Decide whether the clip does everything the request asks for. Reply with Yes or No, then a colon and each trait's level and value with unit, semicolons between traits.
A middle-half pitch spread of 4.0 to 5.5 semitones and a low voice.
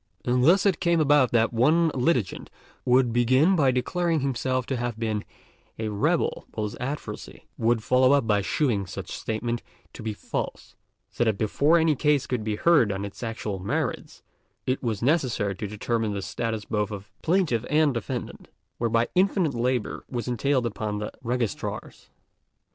Yes: average, 4.5 semitones; low, 120 Hz